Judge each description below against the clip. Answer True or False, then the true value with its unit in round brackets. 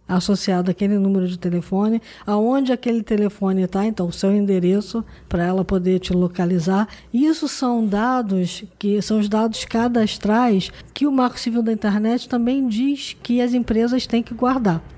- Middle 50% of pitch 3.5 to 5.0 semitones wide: True (3.9 semitones)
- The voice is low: False (215 Hz)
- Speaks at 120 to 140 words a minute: False (160 wpm)